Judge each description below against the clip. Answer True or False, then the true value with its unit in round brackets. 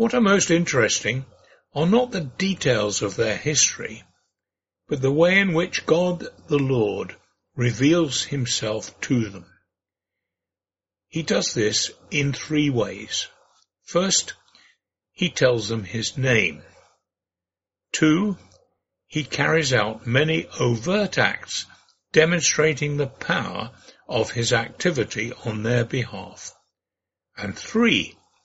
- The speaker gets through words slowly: True (110 wpm)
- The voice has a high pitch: False (135 Hz)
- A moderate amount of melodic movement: False (7.2 semitones)